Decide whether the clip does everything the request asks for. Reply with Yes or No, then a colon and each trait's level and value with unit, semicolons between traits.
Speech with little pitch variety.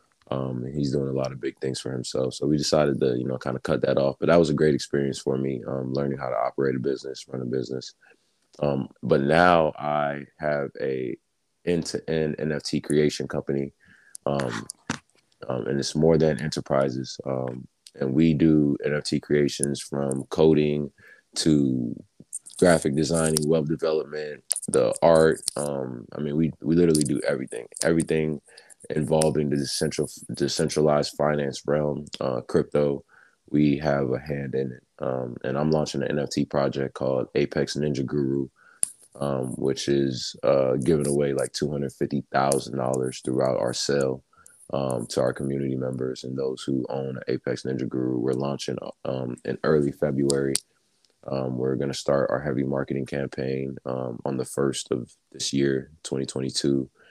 Yes: narrow, 2.1 semitones